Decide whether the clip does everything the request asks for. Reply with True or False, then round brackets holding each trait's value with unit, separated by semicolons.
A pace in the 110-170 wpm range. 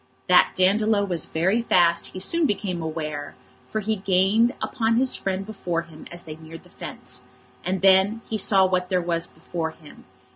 False (180 wpm)